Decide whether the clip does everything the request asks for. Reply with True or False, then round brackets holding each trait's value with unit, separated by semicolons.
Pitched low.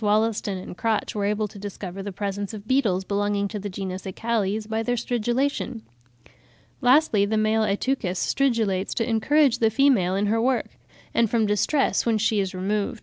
False (215 Hz)